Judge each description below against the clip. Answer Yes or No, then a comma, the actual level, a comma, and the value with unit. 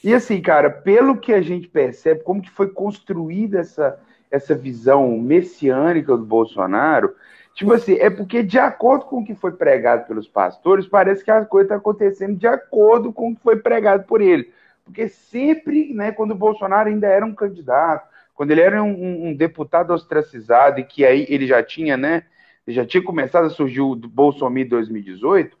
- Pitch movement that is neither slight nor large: No, wide, 7.1 semitones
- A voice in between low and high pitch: No, high, 195 Hz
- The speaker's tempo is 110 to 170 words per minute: No, fast, 185 wpm